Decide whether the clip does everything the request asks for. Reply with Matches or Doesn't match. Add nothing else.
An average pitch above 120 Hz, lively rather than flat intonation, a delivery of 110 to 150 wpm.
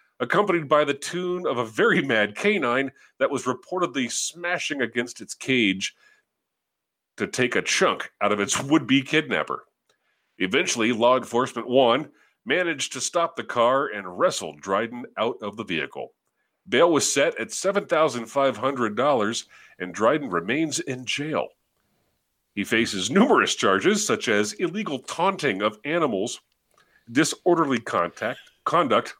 Matches